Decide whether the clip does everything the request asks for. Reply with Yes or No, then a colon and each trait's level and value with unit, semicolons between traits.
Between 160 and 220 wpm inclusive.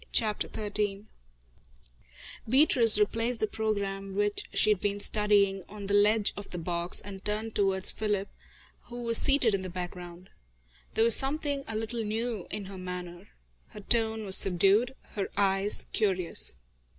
No: average, 150 wpm